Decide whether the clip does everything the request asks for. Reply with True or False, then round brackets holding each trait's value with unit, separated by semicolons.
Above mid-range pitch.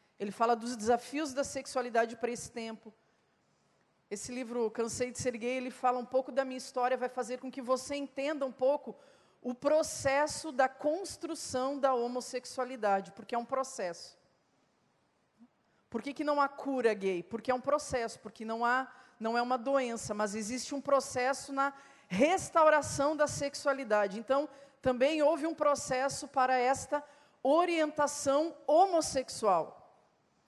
True (260 Hz)